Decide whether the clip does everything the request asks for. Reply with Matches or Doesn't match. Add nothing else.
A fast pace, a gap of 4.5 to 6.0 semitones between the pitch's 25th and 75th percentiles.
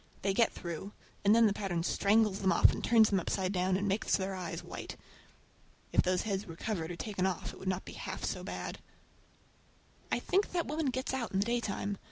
Doesn't match